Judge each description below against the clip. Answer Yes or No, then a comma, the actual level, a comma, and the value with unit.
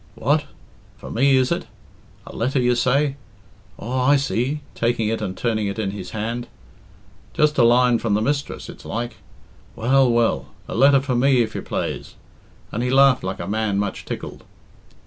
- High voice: No, low, 120 Hz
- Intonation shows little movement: No, average, 3.5 semitones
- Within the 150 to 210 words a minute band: Yes, average, 175 wpm